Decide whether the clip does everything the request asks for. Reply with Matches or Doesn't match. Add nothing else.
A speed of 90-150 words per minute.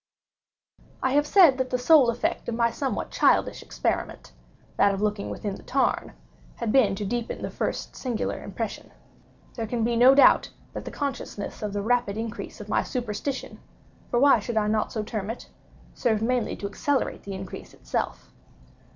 Doesn't match